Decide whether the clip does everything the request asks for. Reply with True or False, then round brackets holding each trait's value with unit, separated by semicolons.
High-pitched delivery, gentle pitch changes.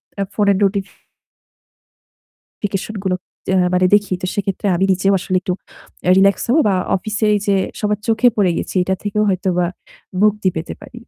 True (200 Hz; 2.1 semitones)